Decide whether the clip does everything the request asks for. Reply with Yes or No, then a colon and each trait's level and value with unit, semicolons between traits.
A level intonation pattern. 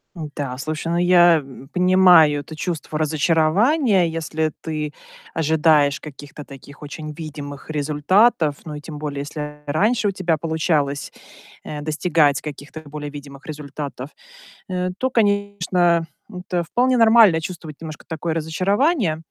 No: average, 3.4 semitones